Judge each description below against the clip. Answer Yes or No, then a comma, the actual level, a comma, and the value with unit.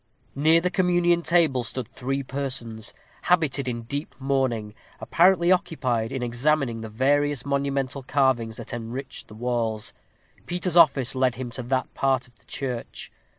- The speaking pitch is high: No, low, 135 Hz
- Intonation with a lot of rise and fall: No, average, 3.4 semitones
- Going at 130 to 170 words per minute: Yes, average, 150 wpm